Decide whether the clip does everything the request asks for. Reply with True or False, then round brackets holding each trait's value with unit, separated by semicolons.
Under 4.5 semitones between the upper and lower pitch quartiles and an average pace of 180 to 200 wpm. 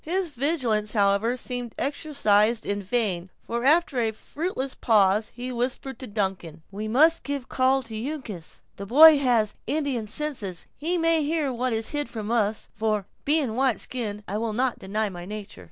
False (5.0 semitones; 185 wpm)